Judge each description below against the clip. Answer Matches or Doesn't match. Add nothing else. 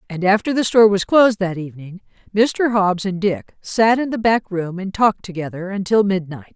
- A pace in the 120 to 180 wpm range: Doesn't match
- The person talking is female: Matches